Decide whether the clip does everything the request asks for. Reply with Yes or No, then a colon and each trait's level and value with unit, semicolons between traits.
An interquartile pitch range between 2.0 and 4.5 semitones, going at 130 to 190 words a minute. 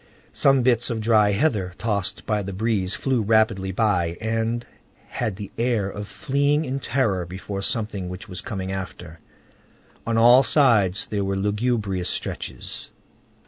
Yes: average, 3.5 semitones; average, 145 wpm